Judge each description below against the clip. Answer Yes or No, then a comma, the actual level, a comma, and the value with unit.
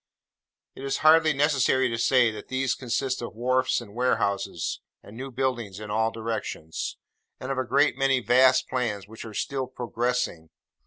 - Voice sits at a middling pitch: No, low, 125 Hz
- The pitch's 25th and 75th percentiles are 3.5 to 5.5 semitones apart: No, average, 2.9 semitones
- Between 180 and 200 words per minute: No, average, 165 wpm